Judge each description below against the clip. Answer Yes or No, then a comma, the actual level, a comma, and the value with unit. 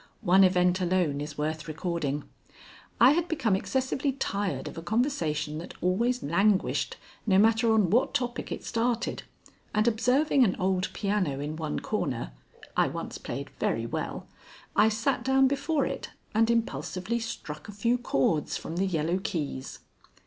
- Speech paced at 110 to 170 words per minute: Yes, average, 155 wpm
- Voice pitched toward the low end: No, high, 195 Hz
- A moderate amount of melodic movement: No, wide, 6.3 semitones